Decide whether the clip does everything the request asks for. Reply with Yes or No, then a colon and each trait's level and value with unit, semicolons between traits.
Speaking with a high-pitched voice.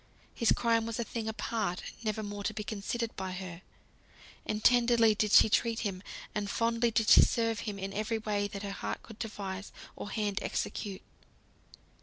Yes: high, 215 Hz